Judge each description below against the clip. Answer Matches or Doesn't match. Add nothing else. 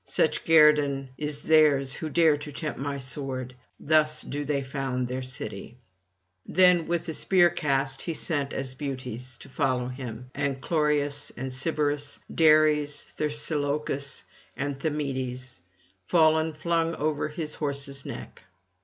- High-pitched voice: Doesn't match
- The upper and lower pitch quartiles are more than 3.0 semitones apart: Doesn't match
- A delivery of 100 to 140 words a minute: Matches